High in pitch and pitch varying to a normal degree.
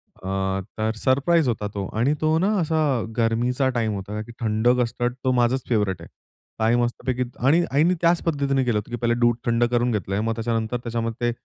No: low, 120 Hz; average, 3.0 semitones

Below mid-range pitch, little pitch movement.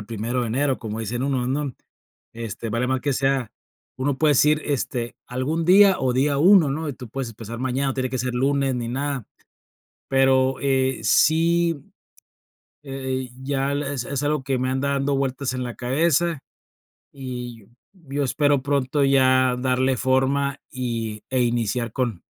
Yes: low, 130 Hz; narrow, 2.2 semitones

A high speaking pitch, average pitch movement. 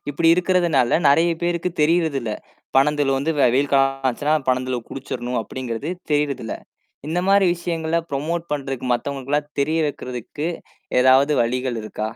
No: medium, 140 Hz; average, 4.1 semitones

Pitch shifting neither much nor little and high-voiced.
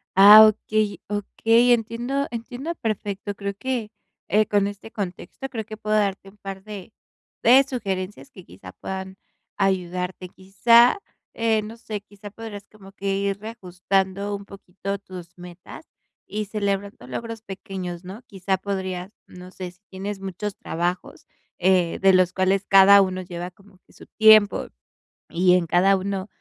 No: narrow, 2.3 semitones; high, 195 Hz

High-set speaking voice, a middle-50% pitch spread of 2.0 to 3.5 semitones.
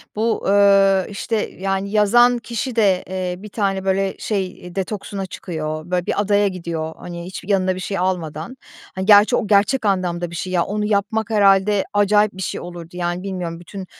Yes: high, 195 Hz; narrow, 2.4 semitones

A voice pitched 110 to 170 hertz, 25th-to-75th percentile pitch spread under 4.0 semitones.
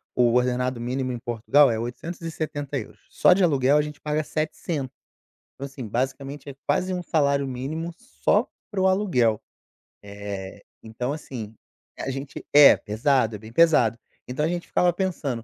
No: low, 135 Hz; average, 4.3 semitones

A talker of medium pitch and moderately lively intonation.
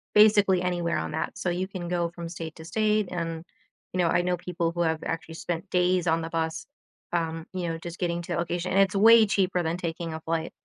No: medium, 175 Hz; narrow, 1.8 semitones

